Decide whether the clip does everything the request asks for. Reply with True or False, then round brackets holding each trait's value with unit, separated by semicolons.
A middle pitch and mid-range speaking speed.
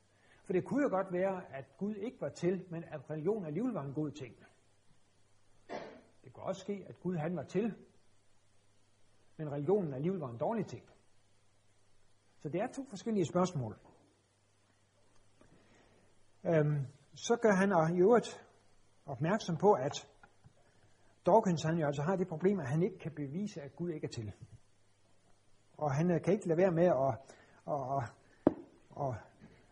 True (150 Hz; 155 wpm)